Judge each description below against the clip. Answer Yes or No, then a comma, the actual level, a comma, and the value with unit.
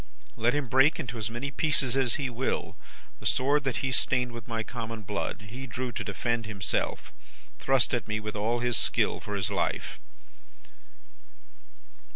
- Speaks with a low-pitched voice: Yes, low, 120 Hz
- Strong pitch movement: No, average, 3.2 semitones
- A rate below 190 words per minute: Yes, average, 170 wpm